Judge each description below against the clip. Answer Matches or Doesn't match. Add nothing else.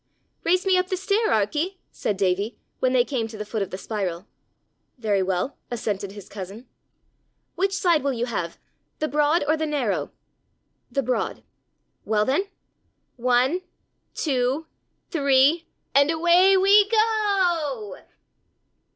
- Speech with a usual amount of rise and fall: Doesn't match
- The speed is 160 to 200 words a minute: Doesn't match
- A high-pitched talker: Matches